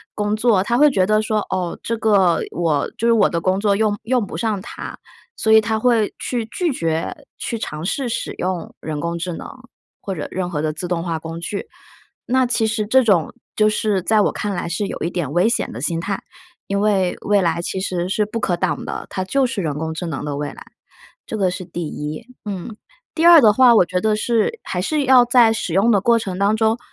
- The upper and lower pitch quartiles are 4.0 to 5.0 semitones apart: Yes, average, 4.3 semitones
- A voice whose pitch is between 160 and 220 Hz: Yes, high, 200 Hz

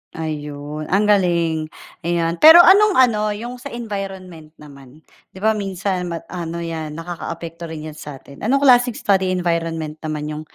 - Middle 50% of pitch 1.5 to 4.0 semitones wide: No, average, 4.6 semitones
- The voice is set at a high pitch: No, medium, 170 Hz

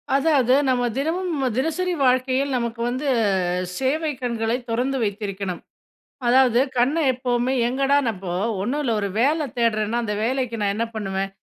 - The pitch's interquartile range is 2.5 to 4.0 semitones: Yes, average, 3.3 semitones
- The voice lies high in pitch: Yes, high, 245 Hz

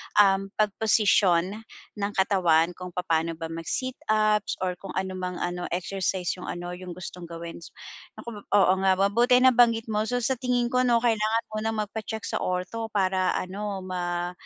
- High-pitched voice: Yes, high, 195 Hz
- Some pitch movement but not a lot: Yes, average, 3.5 semitones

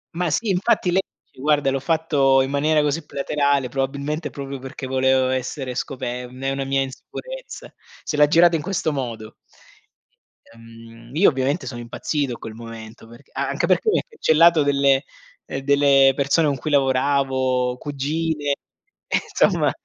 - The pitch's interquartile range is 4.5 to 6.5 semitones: No, narrow, 2.6 semitones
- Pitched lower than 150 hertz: Yes, medium, 140 Hz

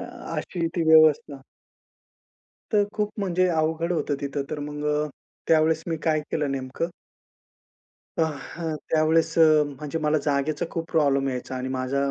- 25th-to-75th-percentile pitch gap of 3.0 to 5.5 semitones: No, narrow, 2.5 semitones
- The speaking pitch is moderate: Yes, medium, 155 Hz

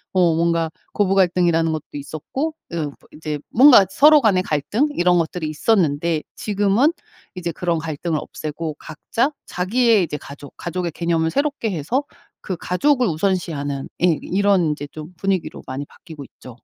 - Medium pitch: Yes, medium, 175 Hz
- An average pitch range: Yes, average, 4.5 semitones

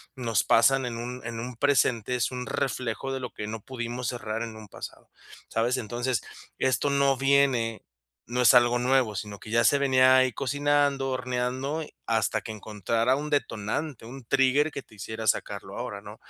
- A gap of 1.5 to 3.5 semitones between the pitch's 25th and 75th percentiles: Yes, average, 2.8 semitones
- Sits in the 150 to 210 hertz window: No, low, 125 Hz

